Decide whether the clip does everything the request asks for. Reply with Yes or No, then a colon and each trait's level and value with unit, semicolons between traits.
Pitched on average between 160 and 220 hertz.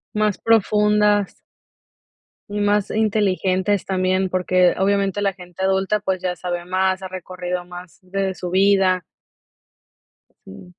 Yes: high, 190 Hz